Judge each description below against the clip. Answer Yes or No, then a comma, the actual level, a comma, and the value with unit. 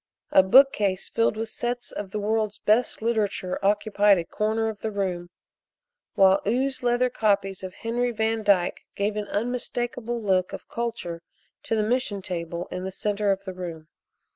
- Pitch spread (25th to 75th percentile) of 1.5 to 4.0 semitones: Yes, average, 3.1 semitones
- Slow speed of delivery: No, average, 165 wpm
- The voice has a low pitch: No, high, 210 Hz